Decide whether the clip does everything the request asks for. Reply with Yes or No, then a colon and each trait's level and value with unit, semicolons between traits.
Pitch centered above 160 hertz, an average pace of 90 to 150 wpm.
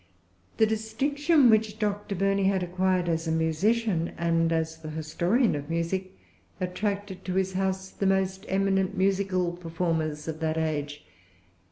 Yes: medium, 185 Hz; average, 145 wpm